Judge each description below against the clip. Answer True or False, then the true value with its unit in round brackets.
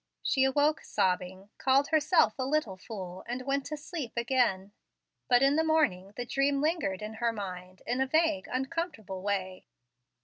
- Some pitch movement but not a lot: False (6.8 semitones)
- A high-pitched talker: True (250 Hz)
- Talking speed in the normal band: True (165 wpm)